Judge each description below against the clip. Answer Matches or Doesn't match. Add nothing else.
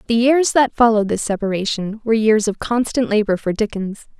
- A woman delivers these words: Matches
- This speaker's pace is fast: Doesn't match